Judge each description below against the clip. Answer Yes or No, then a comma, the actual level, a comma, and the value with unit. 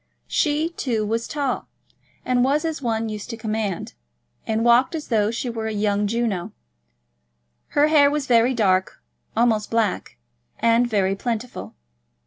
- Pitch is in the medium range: No, high, 230 Hz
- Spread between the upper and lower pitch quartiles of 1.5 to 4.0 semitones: Yes, average, 3.2 semitones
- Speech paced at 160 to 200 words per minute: No, average, 145 wpm